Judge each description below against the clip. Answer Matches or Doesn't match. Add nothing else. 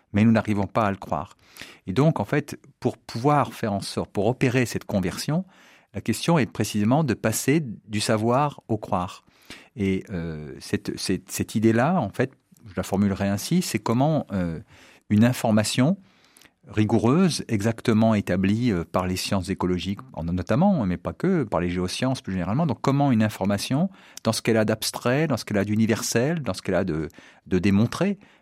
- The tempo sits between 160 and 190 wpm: Matches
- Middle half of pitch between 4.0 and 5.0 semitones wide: Matches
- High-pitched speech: Doesn't match